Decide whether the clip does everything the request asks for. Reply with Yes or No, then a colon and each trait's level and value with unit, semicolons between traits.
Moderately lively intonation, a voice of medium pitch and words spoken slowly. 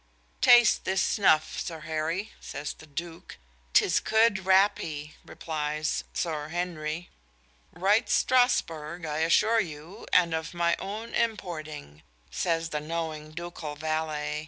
Yes: average, 3.5 semitones; medium, 165 Hz; slow, 120 wpm